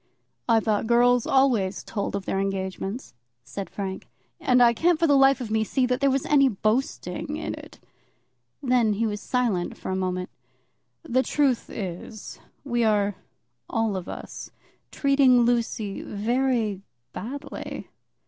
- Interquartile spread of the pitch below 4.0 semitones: No, average, 4.3 semitones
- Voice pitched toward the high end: Yes, high, 230 Hz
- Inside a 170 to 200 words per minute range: No, average, 150 wpm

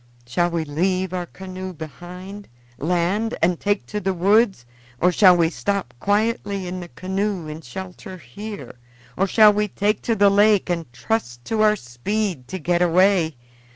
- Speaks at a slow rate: No, average, 165 wpm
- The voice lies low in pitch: No, medium, 185 Hz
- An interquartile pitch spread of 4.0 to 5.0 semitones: No, average, 3.1 semitones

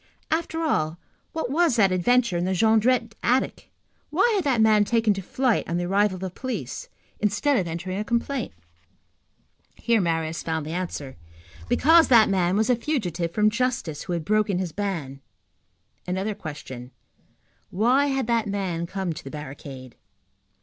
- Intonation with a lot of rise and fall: Yes, wide, 5.8 semitones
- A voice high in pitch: Yes, high, 200 Hz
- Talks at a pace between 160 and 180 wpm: Yes, average, 165 wpm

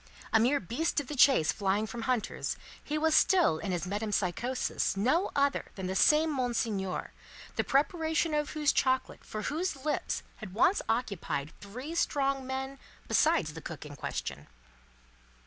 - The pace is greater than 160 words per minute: No, average, 155 wpm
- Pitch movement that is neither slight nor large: No, wide, 7.0 semitones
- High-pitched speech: Yes, very high, 255 Hz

